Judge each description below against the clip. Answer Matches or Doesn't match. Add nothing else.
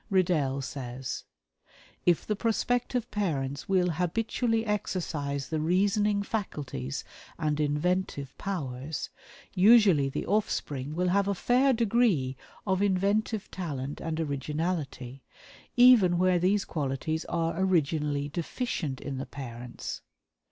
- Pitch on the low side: Doesn't match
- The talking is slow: Matches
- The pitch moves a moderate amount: Doesn't match